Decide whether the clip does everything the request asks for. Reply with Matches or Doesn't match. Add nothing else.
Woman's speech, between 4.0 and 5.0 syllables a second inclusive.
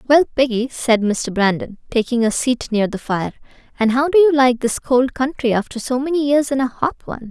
Doesn't match